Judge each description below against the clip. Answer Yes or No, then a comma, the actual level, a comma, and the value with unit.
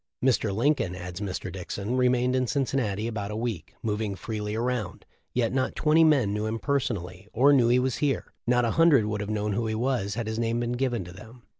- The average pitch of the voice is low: Yes, low, 115 Hz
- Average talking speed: No, fast, 225 wpm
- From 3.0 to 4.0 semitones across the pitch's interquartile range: Yes, average, 3.4 semitones